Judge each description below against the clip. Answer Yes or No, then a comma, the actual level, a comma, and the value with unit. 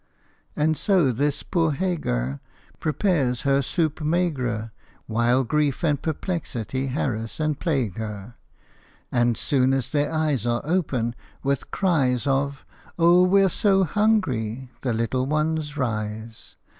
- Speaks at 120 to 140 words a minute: Yes, slow, 135 wpm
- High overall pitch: No, medium, 140 Hz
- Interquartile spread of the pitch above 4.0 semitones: Yes, average, 5.1 semitones